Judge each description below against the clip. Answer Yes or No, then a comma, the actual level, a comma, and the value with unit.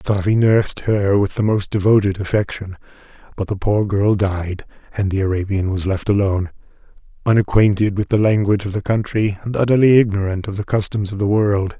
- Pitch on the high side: No, low, 100 Hz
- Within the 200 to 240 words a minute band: No, average, 180 wpm